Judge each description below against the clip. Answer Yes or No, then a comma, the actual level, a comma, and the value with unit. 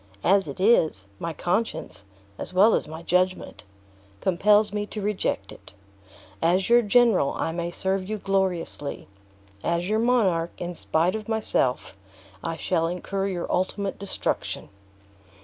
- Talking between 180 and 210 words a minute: No, slow, 135 wpm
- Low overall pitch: No, medium, 185 Hz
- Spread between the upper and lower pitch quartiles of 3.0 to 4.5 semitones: Yes, average, 3.5 semitones